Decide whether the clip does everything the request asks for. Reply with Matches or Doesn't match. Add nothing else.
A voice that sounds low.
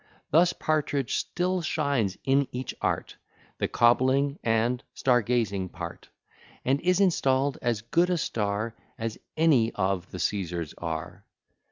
Matches